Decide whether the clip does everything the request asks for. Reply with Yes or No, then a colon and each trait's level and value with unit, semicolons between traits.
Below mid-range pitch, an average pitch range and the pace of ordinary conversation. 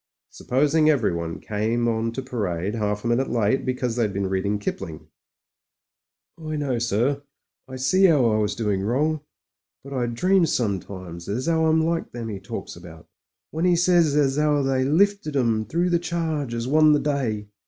No: low, 125 Hz; wide, 6.5 semitones; average, 180 wpm